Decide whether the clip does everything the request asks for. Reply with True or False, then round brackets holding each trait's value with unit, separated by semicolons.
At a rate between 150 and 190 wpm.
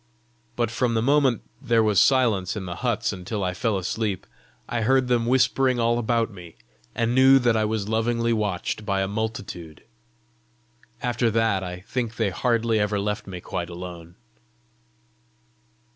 True (160 wpm)